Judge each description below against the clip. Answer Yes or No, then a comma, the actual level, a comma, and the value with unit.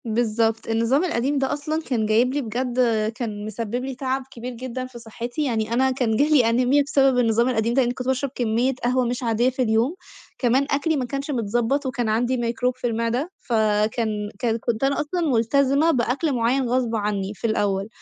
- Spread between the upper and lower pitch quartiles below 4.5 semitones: Yes, average, 2.8 semitones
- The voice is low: No, high, 245 Hz